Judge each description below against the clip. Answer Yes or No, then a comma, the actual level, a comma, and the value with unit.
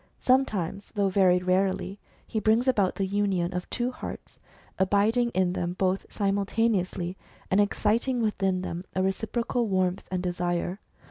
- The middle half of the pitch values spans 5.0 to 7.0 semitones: No, average, 2.9 semitones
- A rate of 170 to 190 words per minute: No, average, 145 wpm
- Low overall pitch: No, high, 195 Hz